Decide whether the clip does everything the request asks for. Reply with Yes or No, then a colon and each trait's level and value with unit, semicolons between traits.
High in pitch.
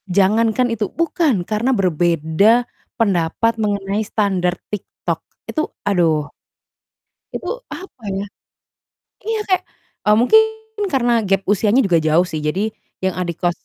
Yes: high, 200 Hz